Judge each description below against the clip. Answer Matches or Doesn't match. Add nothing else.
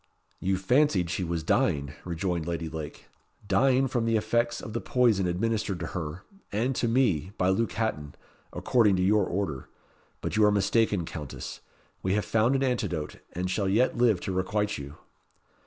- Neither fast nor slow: Matches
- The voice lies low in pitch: Matches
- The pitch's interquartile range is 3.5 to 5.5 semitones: Matches